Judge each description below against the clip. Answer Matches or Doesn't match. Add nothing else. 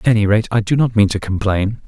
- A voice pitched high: Doesn't match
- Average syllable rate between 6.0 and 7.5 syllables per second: Matches